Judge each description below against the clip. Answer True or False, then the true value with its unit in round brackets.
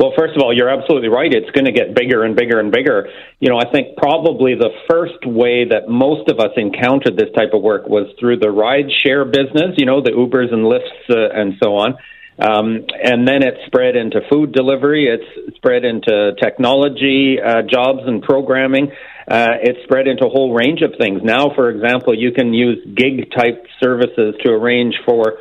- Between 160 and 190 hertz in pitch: False (130 Hz)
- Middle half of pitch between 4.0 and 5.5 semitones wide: False (3.1 semitones)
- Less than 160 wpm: False (205 wpm)